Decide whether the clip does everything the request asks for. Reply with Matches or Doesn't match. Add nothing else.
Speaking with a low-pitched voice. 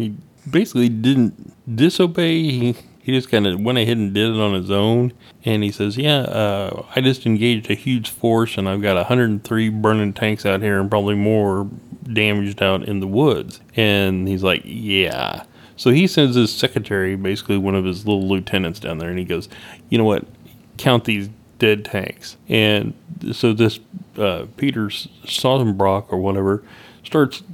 Matches